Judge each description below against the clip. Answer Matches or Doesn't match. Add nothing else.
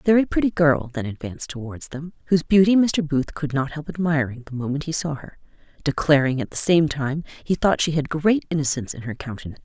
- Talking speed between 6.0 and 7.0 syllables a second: Matches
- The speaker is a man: Doesn't match